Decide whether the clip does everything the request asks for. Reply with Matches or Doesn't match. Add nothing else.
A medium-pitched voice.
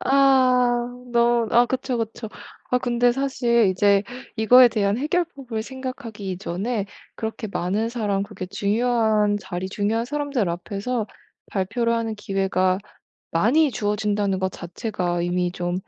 Doesn't match